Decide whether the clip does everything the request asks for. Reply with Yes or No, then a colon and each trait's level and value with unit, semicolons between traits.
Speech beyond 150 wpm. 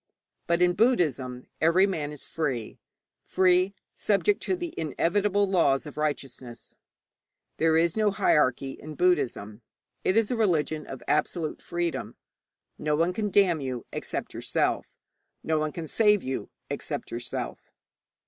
No: average, 140 wpm